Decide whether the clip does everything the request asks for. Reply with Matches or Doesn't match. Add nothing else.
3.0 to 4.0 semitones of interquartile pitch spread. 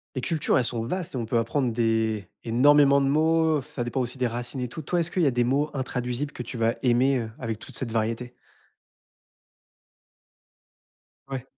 Matches